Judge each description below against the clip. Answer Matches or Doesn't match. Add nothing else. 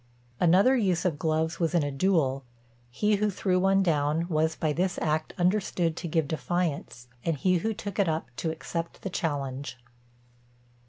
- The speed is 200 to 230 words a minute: Doesn't match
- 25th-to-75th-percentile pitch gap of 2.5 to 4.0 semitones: Matches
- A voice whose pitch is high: Doesn't match